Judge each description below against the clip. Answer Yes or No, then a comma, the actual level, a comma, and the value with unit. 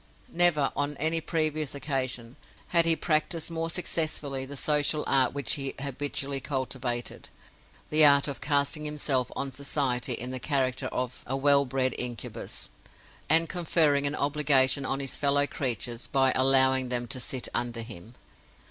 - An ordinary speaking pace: Yes, average, 150 wpm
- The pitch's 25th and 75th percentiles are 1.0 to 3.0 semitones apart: Yes, narrow, 2.6 semitones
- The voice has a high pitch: No, medium, 140 Hz